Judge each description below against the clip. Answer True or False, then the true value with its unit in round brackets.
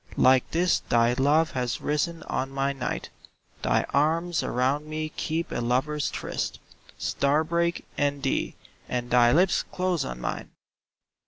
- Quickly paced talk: False (150 wpm)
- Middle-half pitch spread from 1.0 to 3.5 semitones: False (4.0 semitones)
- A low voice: False (145 Hz)